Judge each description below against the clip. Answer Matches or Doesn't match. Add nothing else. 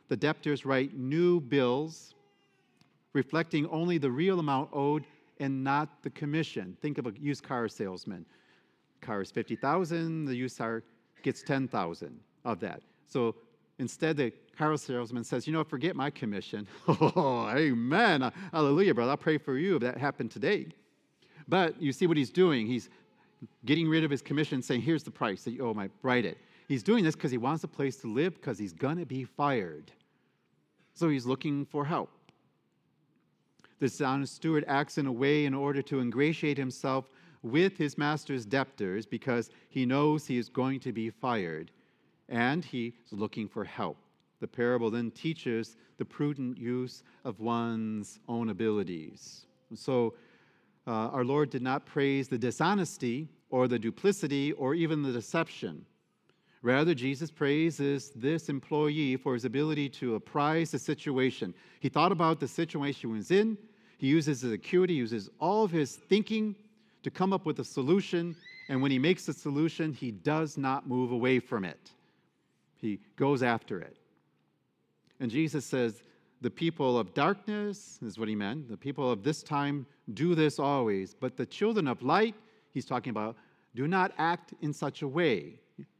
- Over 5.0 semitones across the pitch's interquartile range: Doesn't match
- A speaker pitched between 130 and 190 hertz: Matches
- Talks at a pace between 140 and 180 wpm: Matches